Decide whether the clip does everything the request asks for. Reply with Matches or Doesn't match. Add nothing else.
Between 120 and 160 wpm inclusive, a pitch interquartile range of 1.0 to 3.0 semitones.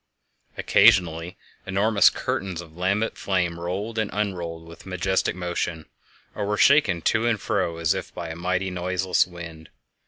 Matches